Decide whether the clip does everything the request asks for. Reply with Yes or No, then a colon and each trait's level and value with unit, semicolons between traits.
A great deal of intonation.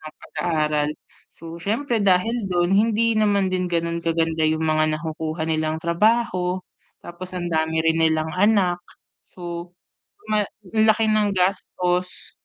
No: average, 3.8 semitones